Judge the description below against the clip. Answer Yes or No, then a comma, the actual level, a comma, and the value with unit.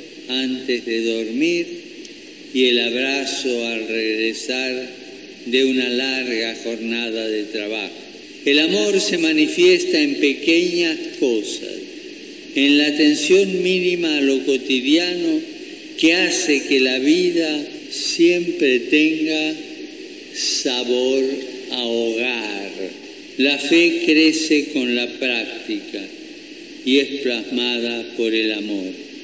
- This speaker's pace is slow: Yes, slow, 105 wpm